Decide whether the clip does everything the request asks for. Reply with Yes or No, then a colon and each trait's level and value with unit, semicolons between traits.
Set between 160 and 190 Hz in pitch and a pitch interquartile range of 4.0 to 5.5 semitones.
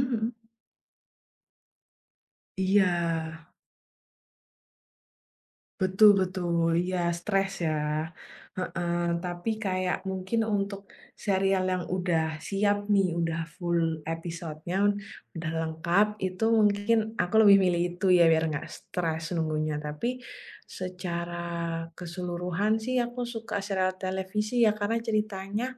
No: medium, 185 Hz; average, 3.1 semitones